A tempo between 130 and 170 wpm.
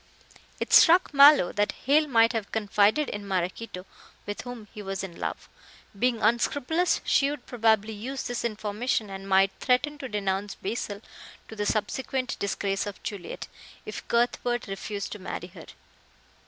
Yes: average, 155 wpm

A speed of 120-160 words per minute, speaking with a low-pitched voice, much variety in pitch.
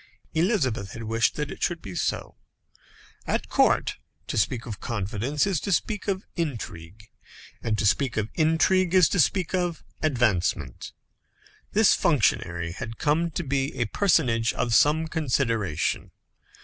Yes: average, 145 wpm; low, 130 Hz; wide, 7.1 semitones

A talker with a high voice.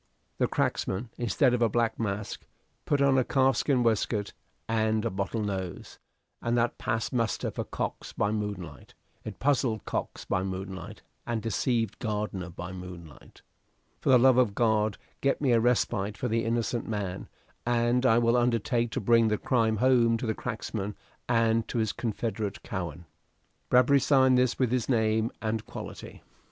No: low, 115 Hz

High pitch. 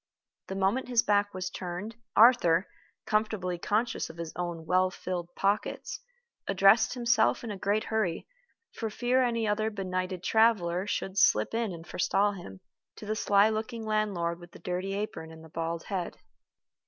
Yes: high, 195 Hz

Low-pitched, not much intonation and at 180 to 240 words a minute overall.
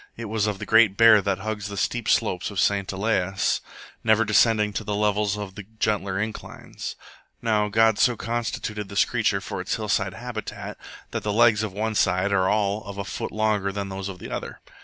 Yes: low, 105 Hz; narrow, 1.8 semitones; average, 200 wpm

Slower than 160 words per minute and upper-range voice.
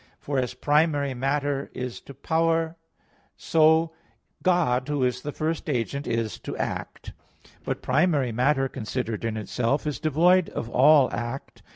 No: average, 145 wpm; medium, 140 Hz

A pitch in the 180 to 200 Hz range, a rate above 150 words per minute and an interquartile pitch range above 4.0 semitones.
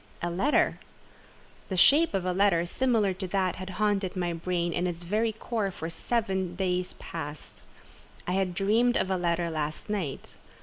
No: medium, 185 Hz; average, 170 wpm; average, 3.0 semitones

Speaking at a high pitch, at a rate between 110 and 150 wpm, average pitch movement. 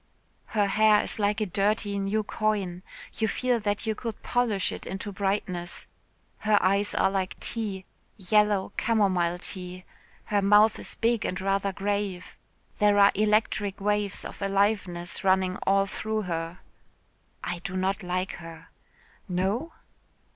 No: high, 200 Hz; average, 140 wpm; narrow, 2.2 semitones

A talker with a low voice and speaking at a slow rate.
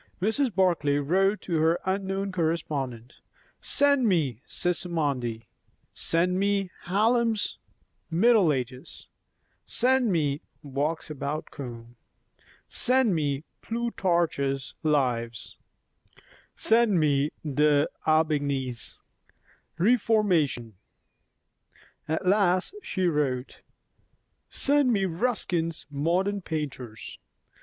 No: medium, 165 Hz; slow, 80 wpm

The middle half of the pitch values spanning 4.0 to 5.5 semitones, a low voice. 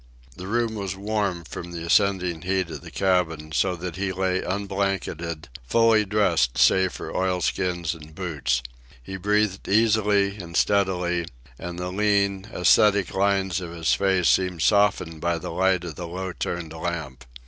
No: narrow, 2.6 semitones; very low, 95 Hz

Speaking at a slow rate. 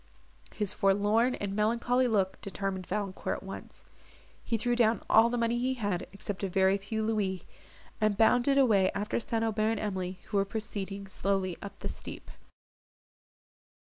No: average, 160 wpm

